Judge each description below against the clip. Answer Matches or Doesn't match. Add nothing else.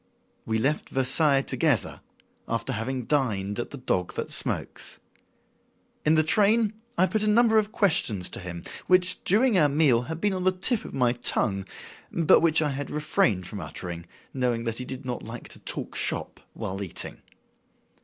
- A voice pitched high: Doesn't match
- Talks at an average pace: Matches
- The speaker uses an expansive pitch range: Matches